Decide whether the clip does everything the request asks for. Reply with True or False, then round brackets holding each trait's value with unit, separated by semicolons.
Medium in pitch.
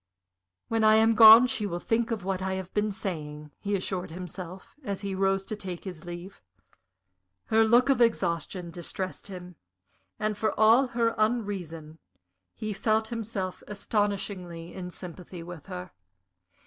False (195 Hz)